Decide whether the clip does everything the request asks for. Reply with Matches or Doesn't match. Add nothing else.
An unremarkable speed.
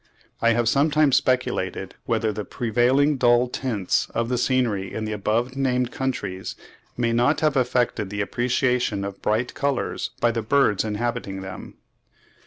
Matches